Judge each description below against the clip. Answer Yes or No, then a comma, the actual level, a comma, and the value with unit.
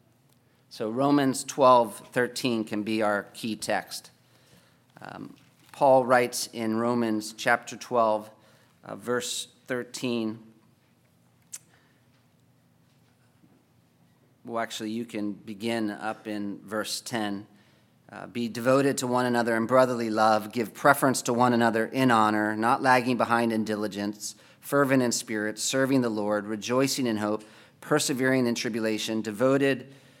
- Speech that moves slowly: Yes, slow, 125 wpm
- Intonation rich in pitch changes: No, average, 2.7 semitones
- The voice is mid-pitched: No, low, 115 Hz